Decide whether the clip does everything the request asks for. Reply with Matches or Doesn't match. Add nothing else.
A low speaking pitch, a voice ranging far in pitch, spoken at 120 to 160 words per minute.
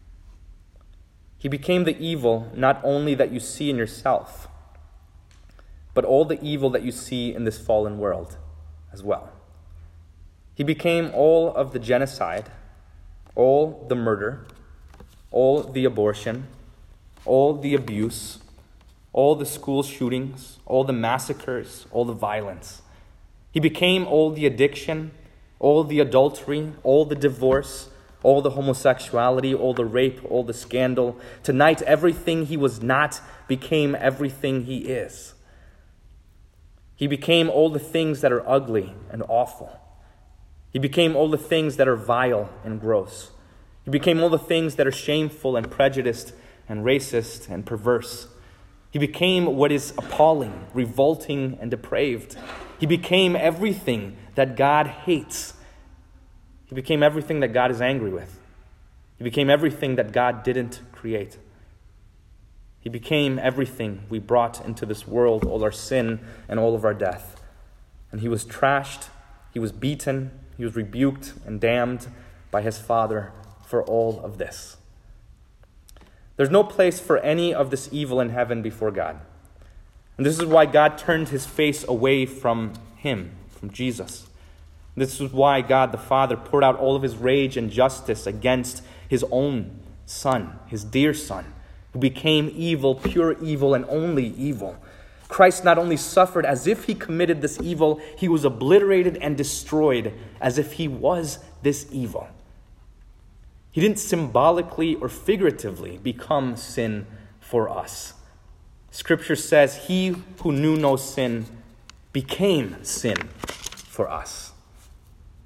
Matches